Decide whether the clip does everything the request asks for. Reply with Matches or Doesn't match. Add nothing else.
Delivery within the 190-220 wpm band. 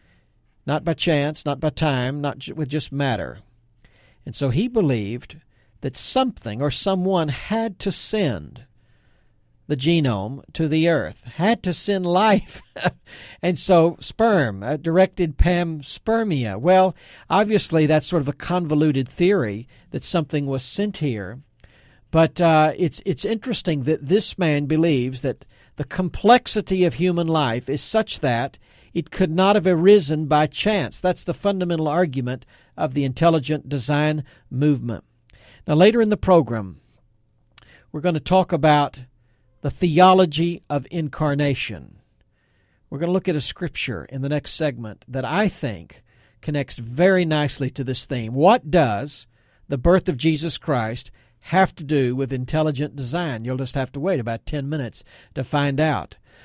Doesn't match